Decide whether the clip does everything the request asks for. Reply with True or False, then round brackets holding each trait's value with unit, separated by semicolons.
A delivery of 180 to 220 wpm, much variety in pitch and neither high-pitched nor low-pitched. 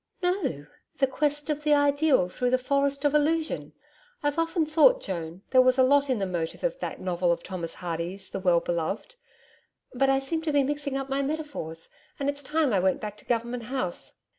False (205 wpm; 7.5 semitones; 270 Hz)